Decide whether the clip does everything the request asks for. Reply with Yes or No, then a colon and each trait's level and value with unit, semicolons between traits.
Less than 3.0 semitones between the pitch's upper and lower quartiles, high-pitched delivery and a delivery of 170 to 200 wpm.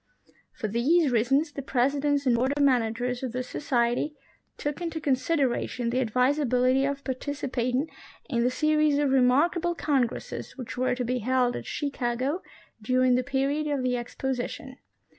No: narrow, 2.6 semitones; very high, 260 Hz; average, 155 wpm